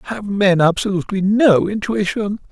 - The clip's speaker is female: No, male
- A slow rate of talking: Yes, slow, 120 wpm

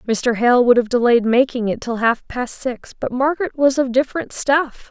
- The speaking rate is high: Yes, fast, 210 wpm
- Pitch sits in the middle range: No, very high, 250 Hz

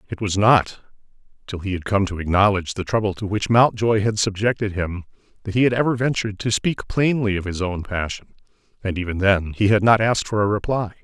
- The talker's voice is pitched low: Yes, low, 105 Hz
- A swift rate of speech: Yes, fast, 210 wpm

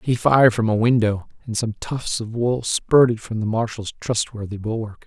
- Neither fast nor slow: Yes, average, 190 wpm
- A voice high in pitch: No, low, 110 Hz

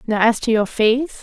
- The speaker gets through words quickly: Yes, fast, 245 wpm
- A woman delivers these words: Yes, female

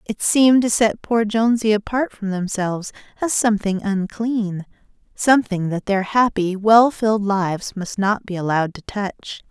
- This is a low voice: No, high, 210 Hz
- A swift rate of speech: No, average, 150 wpm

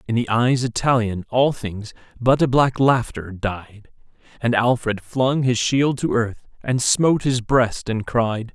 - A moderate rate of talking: Yes, average, 170 wpm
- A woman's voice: No, male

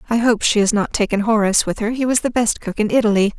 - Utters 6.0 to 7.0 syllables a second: Yes, 6.6 syllables/s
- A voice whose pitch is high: Yes, high, 220 Hz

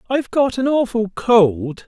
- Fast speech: No, average, 160 wpm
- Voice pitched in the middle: No, high, 225 Hz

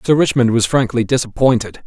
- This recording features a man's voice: Yes, male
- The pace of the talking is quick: No, average, 160 wpm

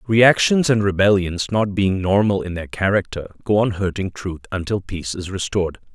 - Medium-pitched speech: No, very low, 95 Hz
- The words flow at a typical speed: Yes, average, 170 wpm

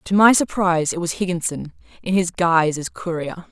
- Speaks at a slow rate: No, average, 170 wpm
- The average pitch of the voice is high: No, medium, 175 Hz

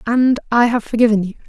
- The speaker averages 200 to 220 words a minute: Yes, fast, 205 wpm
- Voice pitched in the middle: No, high, 230 Hz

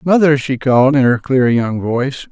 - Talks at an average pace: No, fast, 210 wpm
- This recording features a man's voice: Yes, male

